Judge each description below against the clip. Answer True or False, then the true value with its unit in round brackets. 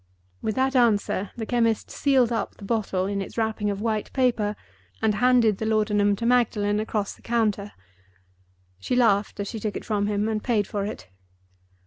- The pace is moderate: True (180 wpm)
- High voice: True (215 Hz)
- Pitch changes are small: True (2.3 semitones)